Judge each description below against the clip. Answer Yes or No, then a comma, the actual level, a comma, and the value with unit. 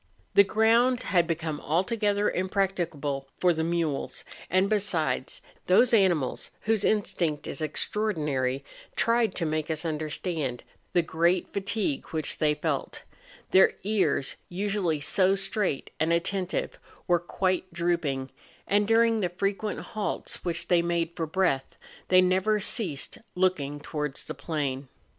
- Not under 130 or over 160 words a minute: Yes, average, 140 wpm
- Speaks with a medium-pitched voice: Yes, medium, 175 Hz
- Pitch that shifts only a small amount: No, average, 4.4 semitones